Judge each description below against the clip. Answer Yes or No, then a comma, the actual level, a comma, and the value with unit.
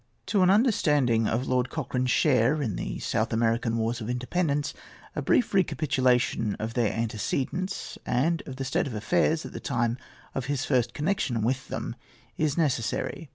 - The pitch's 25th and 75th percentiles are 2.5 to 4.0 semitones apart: No, average, 4.9 semitones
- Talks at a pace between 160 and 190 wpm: Yes, average, 165 wpm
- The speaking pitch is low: Yes, low, 130 Hz